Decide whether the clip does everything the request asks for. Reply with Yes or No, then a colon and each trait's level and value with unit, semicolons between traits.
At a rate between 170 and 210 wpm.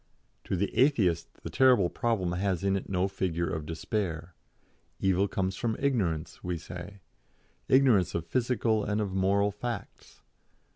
No: average, 145 wpm